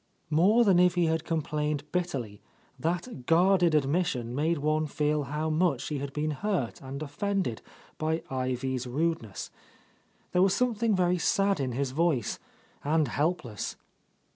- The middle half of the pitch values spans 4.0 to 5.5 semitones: Yes, average, 4.5 semitones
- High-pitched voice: No, medium, 155 Hz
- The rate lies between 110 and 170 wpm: Yes, average, 145 wpm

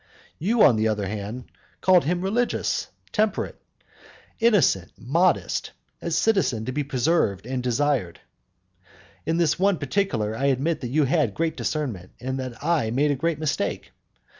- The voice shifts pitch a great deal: Yes, wide, 6.1 semitones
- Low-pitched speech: No, medium, 145 Hz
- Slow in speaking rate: No, average, 150 wpm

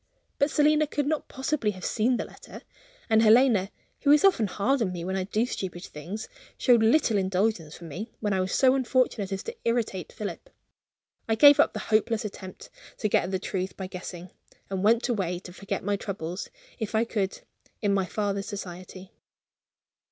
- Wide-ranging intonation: No, average, 4.2 semitones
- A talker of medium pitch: No, high, 210 Hz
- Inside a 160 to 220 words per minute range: Yes, average, 190 wpm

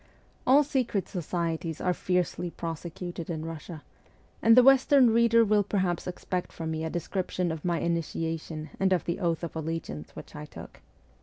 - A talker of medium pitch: Yes, medium, 175 Hz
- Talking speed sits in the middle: Yes, average, 165 wpm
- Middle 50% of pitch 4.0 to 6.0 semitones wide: No, average, 3.3 semitones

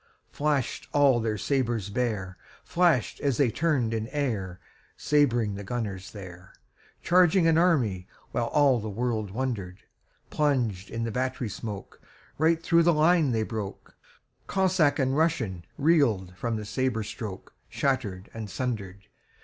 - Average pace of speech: No, slow, 110 wpm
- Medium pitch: No, low, 120 Hz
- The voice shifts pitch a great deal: Yes, wide, 5.9 semitones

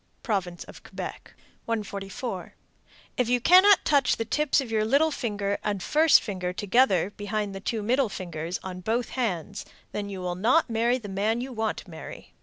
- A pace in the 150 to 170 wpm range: No, average, 180 wpm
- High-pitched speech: Yes, high, 215 Hz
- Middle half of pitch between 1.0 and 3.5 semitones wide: No, average, 4.2 semitones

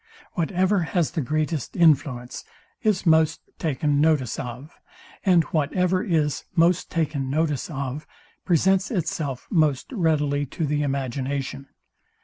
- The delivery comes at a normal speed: No, slow, 120 wpm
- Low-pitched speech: No, medium, 155 Hz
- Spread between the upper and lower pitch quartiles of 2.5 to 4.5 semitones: Yes, average, 3.5 semitones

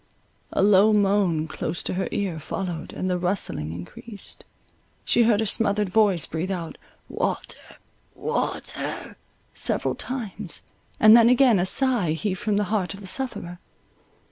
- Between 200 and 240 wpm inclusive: No, average, 145 wpm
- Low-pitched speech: No, high, 195 Hz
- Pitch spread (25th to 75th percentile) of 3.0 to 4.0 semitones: Yes, average, 3.5 semitones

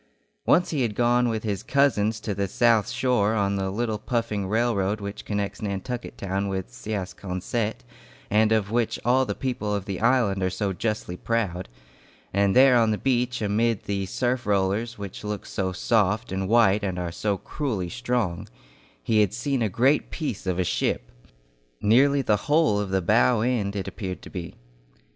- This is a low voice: Yes, low, 105 Hz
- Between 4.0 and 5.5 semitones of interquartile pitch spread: No, average, 3.5 semitones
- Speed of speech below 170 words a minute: No, average, 180 wpm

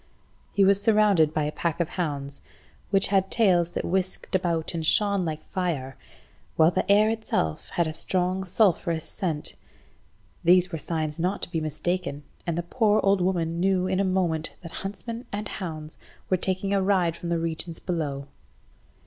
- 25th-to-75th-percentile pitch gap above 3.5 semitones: No, average, 3.2 semitones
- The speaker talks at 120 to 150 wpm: No, average, 175 wpm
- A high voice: No, medium, 180 Hz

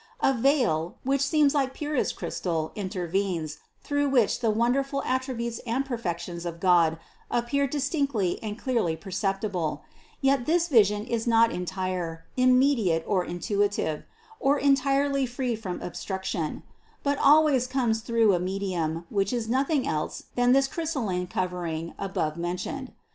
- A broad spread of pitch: Yes, wide, 7.0 semitones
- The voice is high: Yes, high, 225 Hz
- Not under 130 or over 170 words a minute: Yes, slow, 135 wpm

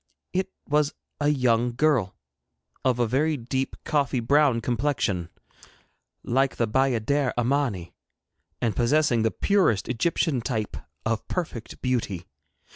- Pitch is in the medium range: No, low, 125 Hz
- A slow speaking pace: Yes, slow, 120 wpm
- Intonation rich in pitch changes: No, average, 4.1 semitones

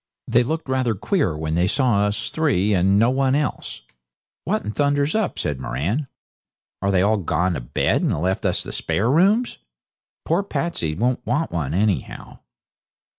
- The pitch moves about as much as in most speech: No, wide, 7.9 semitones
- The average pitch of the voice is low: Yes, low, 110 Hz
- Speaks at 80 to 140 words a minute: No, average, 170 wpm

